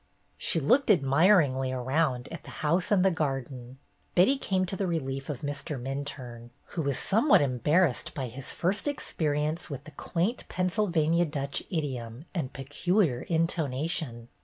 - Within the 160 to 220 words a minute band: No, average, 145 wpm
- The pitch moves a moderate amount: Yes, average, 4.8 semitones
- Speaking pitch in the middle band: Yes, medium, 150 Hz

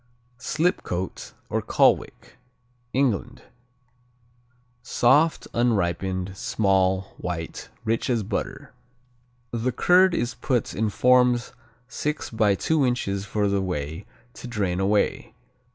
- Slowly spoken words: Yes, slow, 105 wpm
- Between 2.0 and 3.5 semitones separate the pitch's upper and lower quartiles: No, average, 4.6 semitones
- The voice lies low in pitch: Yes, low, 110 Hz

